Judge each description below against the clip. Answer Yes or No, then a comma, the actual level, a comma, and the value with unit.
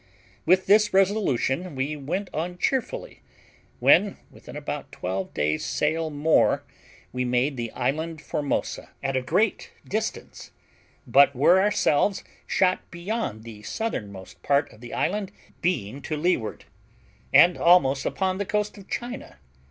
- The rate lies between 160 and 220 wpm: No, slow, 135 wpm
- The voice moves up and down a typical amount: No, wide, 6.7 semitones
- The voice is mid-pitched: Yes, medium, 160 Hz